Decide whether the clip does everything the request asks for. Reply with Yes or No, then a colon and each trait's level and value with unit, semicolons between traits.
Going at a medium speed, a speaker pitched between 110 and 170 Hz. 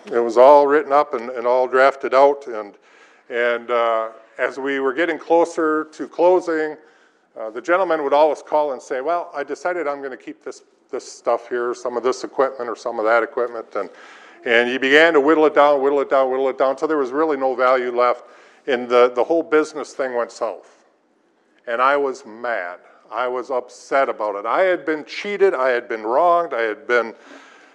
No: fast, 210 wpm; medium, 140 Hz